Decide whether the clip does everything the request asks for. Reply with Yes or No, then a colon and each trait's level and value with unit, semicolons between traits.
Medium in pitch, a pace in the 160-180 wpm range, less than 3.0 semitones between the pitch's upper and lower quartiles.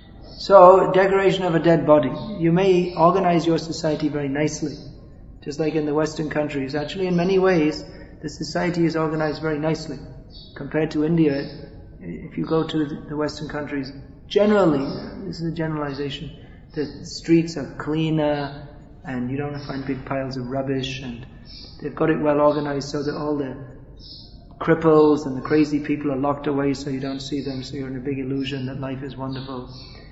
Yes: medium, 150 Hz; average, 175 wpm; narrow, 2.4 semitones